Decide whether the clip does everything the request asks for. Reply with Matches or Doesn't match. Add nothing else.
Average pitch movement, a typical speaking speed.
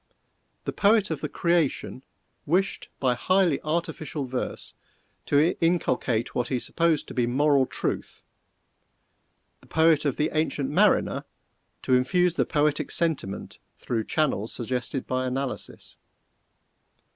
Doesn't match